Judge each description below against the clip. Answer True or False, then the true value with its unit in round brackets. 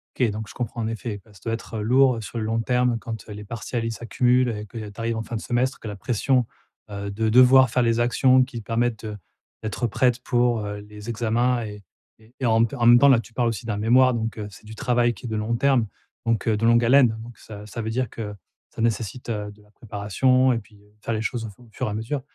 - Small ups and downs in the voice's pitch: True (2.3 semitones)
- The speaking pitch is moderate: False (115 Hz)